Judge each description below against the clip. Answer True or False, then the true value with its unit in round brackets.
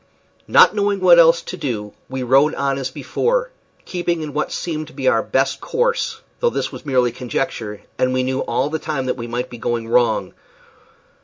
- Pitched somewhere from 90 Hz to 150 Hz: True (135 Hz)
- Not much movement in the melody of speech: False (5.2 semitones)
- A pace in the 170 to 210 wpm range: True (185 wpm)